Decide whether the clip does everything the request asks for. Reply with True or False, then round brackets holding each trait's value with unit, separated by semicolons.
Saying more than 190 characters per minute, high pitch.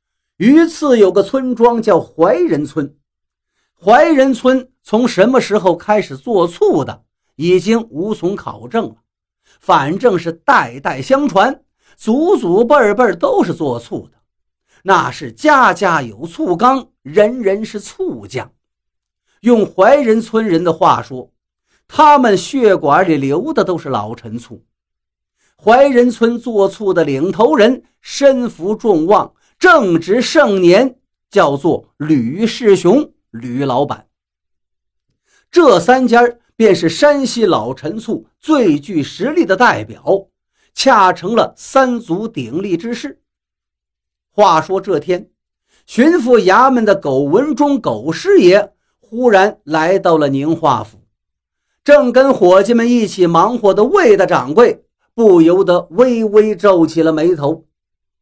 False (180 characters per minute; 210 Hz)